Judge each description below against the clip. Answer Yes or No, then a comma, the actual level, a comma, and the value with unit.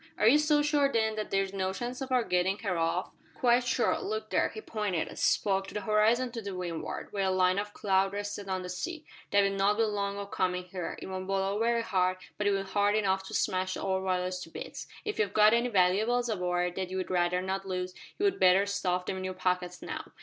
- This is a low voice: No, high, 195 Hz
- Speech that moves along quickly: Yes, fast, 240 wpm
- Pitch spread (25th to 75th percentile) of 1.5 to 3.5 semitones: Yes, average, 2.8 semitones